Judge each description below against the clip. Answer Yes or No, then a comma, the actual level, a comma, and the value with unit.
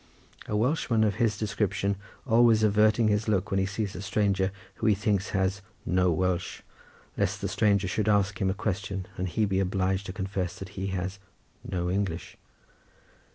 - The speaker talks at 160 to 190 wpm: Yes, average, 175 wpm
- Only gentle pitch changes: Yes, narrow, 2.0 semitones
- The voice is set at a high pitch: No, low, 100 Hz